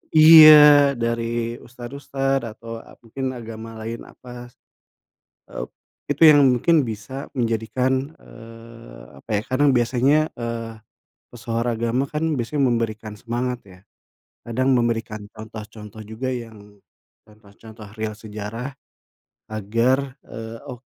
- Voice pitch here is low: Yes, low, 115 Hz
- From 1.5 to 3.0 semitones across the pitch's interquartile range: Yes, average, 2.7 semitones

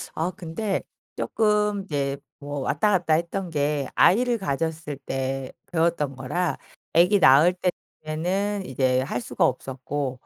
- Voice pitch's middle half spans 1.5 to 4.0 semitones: No, average, 5.2 semitones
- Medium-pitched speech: Yes, medium, 155 Hz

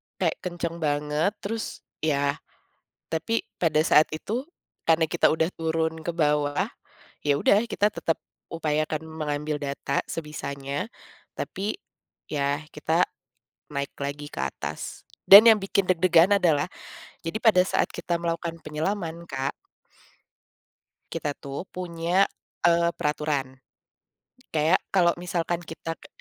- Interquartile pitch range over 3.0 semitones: No, average, 2.7 semitones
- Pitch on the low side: No, medium, 160 Hz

